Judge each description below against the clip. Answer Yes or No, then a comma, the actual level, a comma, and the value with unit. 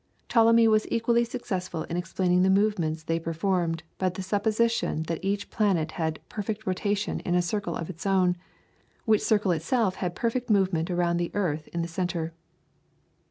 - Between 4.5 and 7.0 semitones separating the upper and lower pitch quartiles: No, average, 3.8 semitones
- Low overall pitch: No, medium, 185 Hz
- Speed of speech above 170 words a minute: No, average, 165 wpm